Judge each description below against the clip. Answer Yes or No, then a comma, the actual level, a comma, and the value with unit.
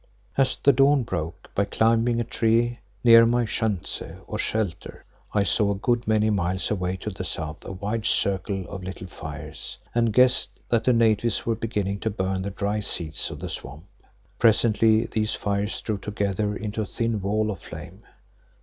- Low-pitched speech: Yes, low, 105 Hz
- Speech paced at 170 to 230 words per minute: Yes, average, 175 wpm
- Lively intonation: No, average, 3.3 semitones